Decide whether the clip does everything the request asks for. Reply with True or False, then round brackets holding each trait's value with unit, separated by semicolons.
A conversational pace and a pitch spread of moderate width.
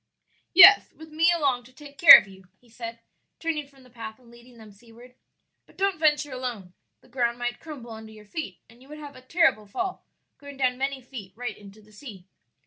False (215 wpm; 4.6 semitones)